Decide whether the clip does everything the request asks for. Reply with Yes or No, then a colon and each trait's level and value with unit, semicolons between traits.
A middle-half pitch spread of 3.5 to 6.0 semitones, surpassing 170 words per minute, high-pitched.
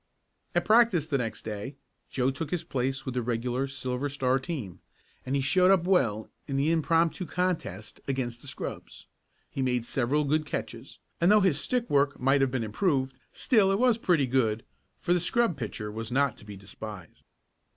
No: wide, 5.5 semitones; average, 185 wpm; low, 135 Hz